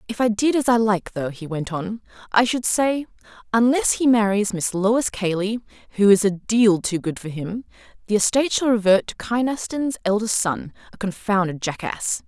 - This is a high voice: Yes, high, 215 Hz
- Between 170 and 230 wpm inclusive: Yes, average, 185 wpm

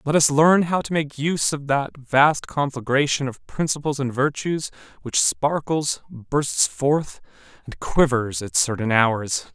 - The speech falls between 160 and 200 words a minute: No, average, 150 wpm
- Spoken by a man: Yes, male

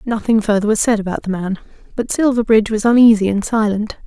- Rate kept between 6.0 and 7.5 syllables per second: Yes, 6.3 syllables/s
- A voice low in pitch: No, high, 215 Hz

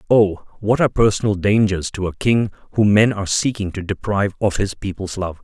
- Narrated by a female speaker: No, male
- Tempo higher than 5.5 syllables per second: Yes, 5.7 syllables/s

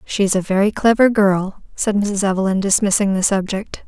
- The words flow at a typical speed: Yes, average, 170 wpm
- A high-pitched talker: Yes, high, 200 Hz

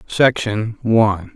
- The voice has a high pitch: No, low, 110 Hz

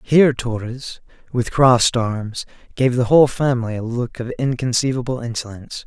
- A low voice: Yes, low, 120 Hz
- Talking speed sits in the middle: Yes, average, 145 wpm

